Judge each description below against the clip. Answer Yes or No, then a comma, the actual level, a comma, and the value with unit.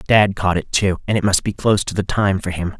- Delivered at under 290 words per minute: No, fast, 300 wpm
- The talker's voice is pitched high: No, very low, 95 Hz